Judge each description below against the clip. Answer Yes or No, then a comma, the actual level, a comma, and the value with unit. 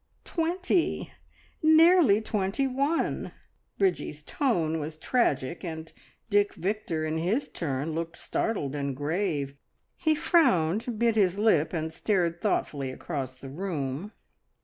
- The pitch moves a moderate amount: No, wide, 6.5 semitones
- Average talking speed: No, slow, 120 wpm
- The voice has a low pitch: No, medium, 180 Hz